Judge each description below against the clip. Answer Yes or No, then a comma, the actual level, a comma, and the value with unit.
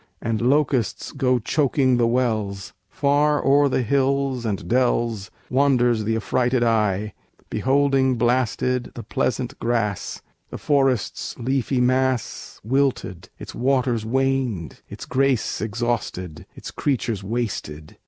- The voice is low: Yes, low, 125 Hz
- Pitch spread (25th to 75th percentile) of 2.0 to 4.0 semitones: Yes, average, 3.1 semitones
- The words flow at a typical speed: No, slow, 115 wpm